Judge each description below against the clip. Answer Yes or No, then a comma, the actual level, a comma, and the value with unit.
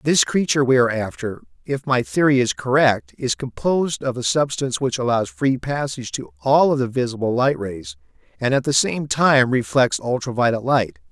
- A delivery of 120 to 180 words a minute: No, average, 190 wpm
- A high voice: No, low, 130 Hz